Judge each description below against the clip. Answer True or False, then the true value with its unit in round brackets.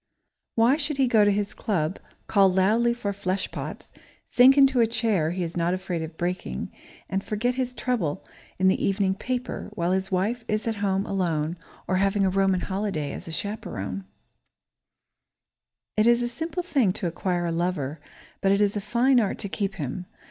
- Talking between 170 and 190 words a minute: True (185 wpm)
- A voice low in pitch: False (195 Hz)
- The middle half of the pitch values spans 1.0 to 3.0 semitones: False (4.2 semitones)